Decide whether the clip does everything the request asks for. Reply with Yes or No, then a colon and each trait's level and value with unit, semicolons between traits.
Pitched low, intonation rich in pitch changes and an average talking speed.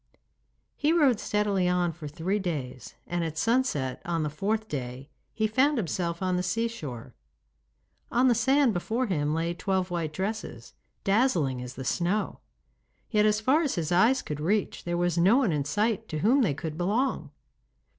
No: medium, 185 Hz; wide, 5.8 semitones; average, 175 wpm